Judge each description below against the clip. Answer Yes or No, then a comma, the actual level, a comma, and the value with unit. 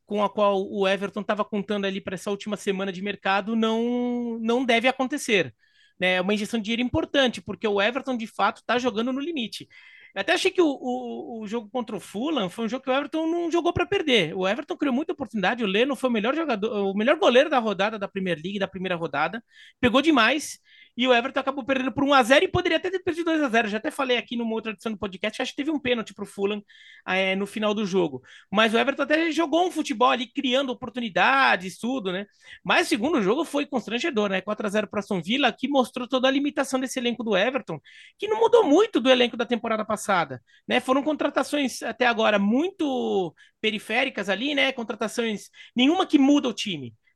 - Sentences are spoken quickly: Yes, fast, 220 wpm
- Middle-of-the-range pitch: No, high, 240 Hz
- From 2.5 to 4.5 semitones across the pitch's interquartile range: No, average, 5.0 semitones